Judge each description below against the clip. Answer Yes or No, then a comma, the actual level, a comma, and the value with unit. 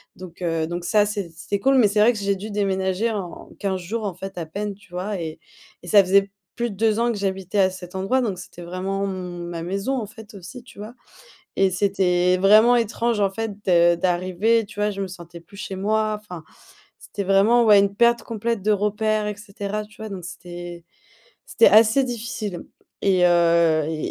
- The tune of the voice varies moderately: Yes, average, 3.0 semitones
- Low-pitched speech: No, high, 200 Hz